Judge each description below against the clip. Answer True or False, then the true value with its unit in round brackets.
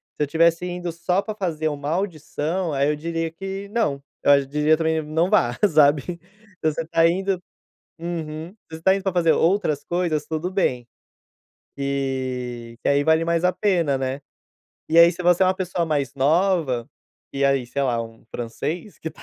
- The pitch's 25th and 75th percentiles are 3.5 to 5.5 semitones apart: True (4.0 semitones)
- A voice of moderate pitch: True (160 Hz)